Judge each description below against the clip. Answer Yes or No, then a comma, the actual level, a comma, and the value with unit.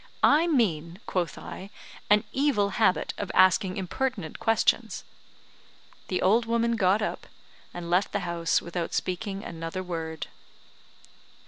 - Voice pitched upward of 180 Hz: Yes, high, 190 Hz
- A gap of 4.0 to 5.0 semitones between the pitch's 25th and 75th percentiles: Yes, average, 4.3 semitones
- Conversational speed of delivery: No, slow, 125 wpm